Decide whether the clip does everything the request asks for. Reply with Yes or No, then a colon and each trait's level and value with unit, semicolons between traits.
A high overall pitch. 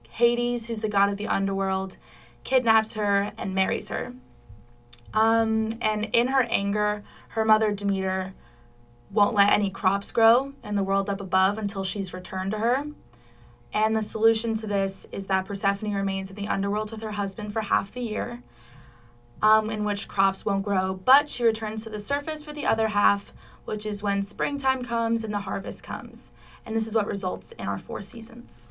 Yes: high, 210 Hz